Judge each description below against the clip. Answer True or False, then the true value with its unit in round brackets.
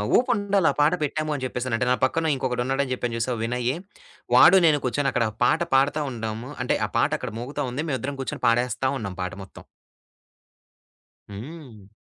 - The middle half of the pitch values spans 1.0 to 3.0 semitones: False (3.9 semitones)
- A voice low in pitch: True (130 Hz)